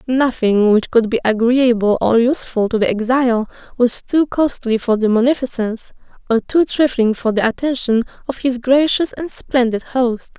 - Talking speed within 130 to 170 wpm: Yes, average, 160 wpm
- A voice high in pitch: Yes, high, 240 Hz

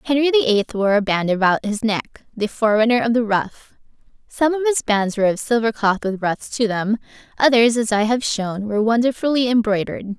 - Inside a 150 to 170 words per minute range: No, average, 200 wpm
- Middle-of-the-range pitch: No, high, 225 Hz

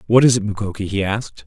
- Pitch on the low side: Yes, low, 105 Hz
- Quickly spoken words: Yes, fast, 245 wpm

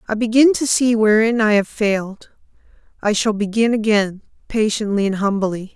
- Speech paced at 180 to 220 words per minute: No, average, 155 wpm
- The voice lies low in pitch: No, high, 215 Hz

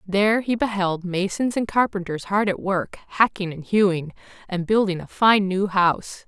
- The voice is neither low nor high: No, high, 195 Hz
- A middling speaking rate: Yes, average, 170 wpm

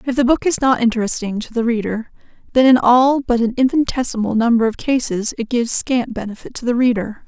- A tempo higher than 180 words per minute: Yes, fast, 205 wpm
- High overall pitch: Yes, high, 240 Hz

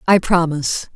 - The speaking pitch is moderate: Yes, medium, 170 Hz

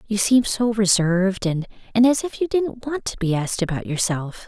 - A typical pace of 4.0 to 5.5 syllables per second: Yes, 5.2 syllables/s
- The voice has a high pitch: Yes, high, 210 Hz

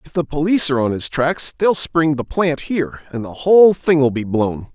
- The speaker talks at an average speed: No, fast, 230 wpm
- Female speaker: No, male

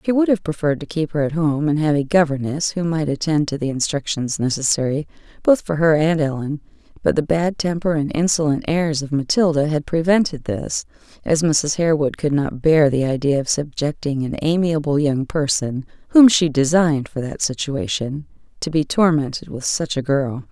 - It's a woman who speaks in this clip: Yes, female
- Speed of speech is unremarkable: Yes, average, 185 wpm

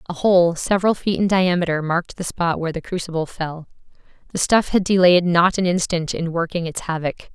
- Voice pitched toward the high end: No, medium, 175 Hz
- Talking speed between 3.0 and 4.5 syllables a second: No, 5.7 syllables/s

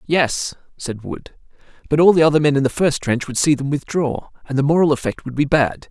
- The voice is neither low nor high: Yes, medium, 145 Hz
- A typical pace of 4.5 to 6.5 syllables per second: Yes, 5.5 syllables/s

